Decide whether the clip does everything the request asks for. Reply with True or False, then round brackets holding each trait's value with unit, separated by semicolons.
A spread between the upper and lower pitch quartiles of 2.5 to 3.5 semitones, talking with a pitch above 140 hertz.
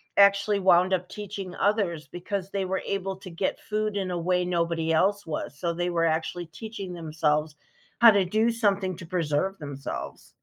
True (2.9 semitones; 185 Hz)